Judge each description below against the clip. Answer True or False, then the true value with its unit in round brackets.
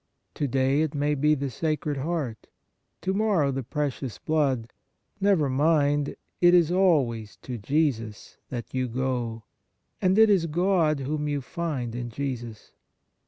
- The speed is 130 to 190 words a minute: True (145 wpm)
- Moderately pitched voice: True (145 Hz)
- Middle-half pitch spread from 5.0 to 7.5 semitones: False (4.1 semitones)